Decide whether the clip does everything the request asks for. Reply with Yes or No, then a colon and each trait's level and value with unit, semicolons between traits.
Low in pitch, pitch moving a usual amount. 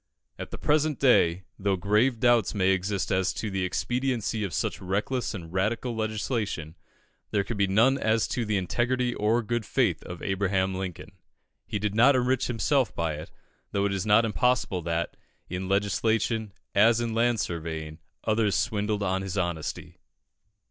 Yes: low, 105 Hz; average, 3.6 semitones